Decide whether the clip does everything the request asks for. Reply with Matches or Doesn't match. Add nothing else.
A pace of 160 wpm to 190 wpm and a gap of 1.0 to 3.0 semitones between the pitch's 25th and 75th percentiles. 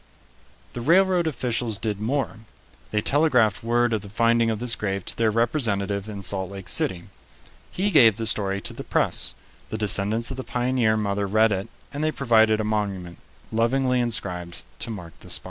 Doesn't match